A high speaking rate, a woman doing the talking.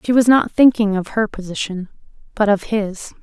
No: average, 185 wpm; female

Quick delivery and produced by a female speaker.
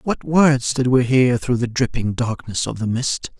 No: fast, 210 wpm; male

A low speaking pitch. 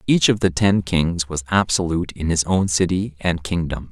Yes: very low, 85 Hz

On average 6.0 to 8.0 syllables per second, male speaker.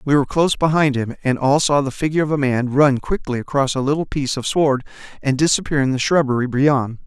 Yes: 6.2 syllables/s; male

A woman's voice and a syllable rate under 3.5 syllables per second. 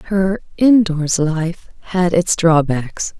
Yes: female; 2.9 syllables/s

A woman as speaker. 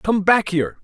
No: male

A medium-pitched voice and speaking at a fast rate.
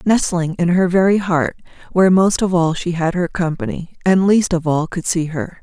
Yes: medium, 175 Hz; fast, 215 wpm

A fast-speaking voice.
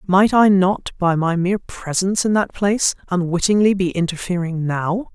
No: average, 165 wpm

